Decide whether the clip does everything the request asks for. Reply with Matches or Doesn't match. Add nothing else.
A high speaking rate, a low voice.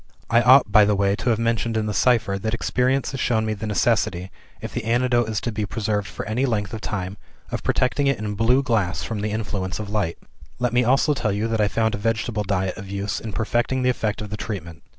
Matches